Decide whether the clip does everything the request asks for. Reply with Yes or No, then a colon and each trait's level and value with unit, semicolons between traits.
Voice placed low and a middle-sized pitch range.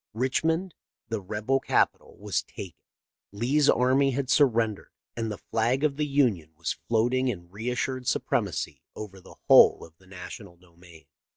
No: low, 115 Hz; wide, 5.9 semitones